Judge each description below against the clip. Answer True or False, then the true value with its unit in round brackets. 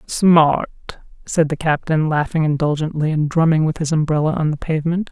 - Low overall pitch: False (155 Hz)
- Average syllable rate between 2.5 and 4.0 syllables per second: False (5.4 syllables/s)